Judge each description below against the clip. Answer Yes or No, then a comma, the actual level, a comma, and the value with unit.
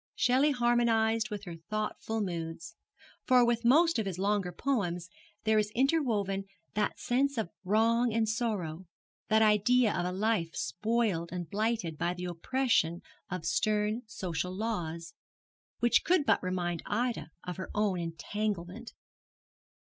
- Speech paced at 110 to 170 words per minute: Yes, average, 140 wpm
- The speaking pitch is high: Yes, high, 210 Hz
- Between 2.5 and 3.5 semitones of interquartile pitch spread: No, average, 4.7 semitones